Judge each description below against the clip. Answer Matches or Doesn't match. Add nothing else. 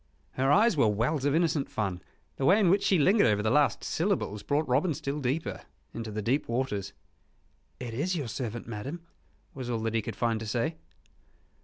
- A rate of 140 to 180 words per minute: Doesn't match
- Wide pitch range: Matches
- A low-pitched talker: Matches